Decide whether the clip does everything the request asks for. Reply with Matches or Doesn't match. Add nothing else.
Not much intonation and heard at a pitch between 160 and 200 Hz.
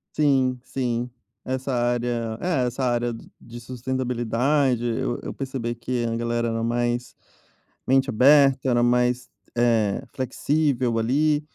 Doesn't match